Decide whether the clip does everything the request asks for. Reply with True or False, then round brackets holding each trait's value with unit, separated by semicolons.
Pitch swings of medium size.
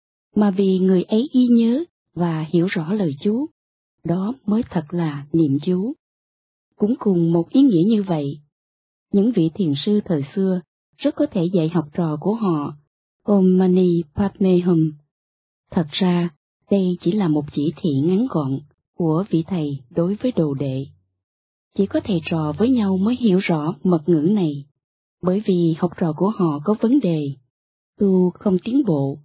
True (4.5 semitones)